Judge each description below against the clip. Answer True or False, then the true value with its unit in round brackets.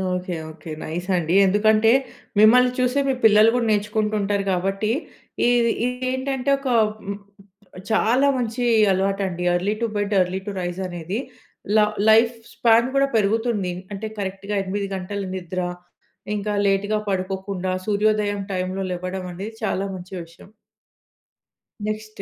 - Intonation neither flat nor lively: True (3.0 semitones)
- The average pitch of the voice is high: True (205 Hz)